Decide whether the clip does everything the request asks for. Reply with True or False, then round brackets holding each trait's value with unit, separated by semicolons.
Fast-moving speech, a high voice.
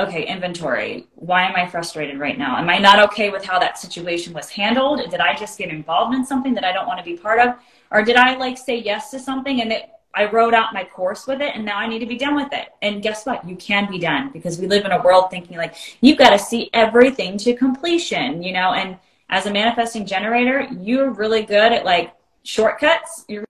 True (245 wpm; 210 Hz)